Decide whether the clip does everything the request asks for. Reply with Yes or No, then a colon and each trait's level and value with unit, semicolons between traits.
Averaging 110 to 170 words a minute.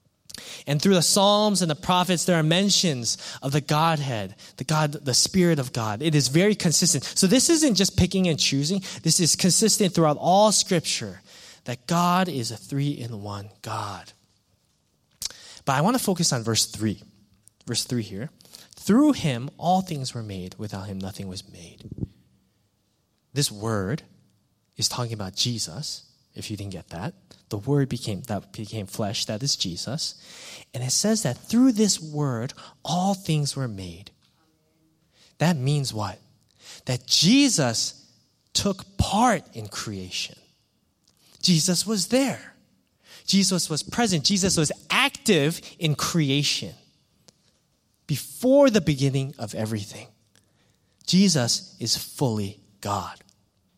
Yes: average, 140 wpm